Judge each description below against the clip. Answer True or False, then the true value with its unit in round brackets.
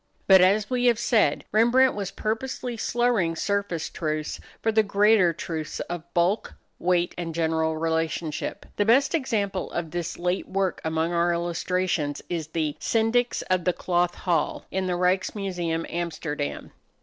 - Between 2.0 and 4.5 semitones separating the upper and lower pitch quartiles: True (4.0 semitones)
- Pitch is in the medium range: True (180 Hz)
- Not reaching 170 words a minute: True (150 wpm)